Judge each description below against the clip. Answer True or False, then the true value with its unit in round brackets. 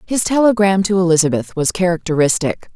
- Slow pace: True (130 wpm)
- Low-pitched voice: False (185 Hz)